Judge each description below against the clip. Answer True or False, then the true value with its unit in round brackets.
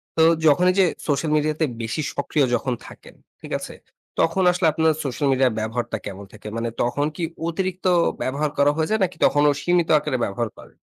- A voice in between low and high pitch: True (145 Hz)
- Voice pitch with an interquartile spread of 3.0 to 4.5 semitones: False (4.9 semitones)